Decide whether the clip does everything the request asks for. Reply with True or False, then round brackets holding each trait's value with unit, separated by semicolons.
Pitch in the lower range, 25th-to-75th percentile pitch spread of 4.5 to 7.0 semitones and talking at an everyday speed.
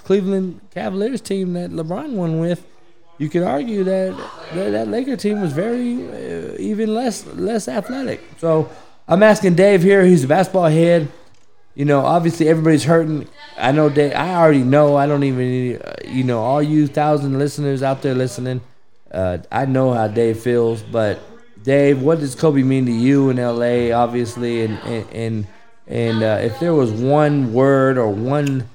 False (145 Hz; 5.6 semitones; 170 wpm)